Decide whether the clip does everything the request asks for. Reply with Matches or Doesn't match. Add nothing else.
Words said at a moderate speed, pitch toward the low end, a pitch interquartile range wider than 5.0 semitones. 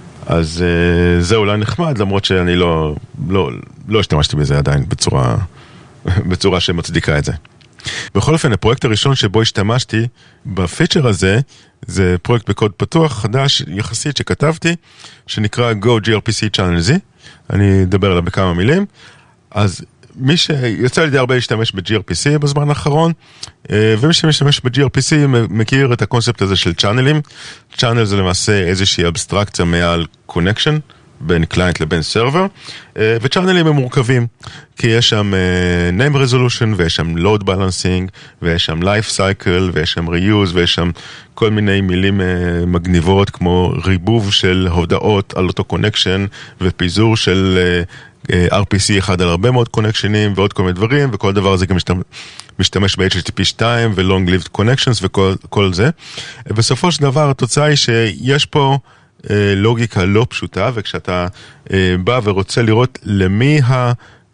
Matches